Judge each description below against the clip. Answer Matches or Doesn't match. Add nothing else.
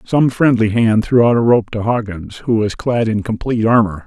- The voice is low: Matches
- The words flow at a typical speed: Doesn't match